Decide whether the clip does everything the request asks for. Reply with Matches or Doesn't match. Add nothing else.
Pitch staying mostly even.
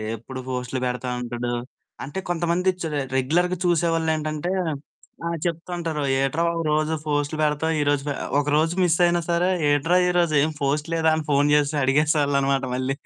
Doesn't match